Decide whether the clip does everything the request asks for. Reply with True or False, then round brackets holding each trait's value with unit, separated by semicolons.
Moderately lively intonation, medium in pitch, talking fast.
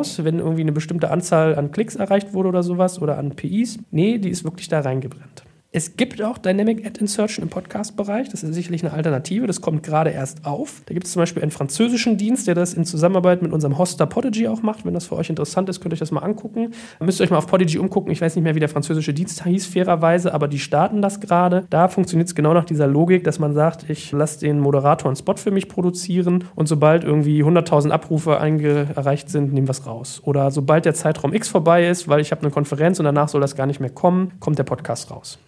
True (3.8 semitones; 165 Hz; 245 wpm)